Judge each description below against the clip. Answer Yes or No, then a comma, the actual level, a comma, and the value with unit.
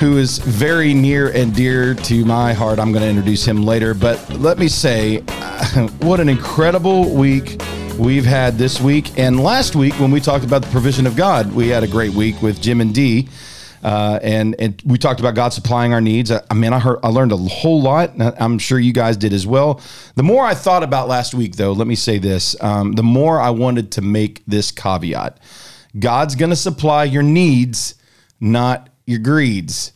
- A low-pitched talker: Yes, low, 120 Hz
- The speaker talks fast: Yes, fast, 210 wpm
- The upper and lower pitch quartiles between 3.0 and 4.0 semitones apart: Yes, average, 3.7 semitones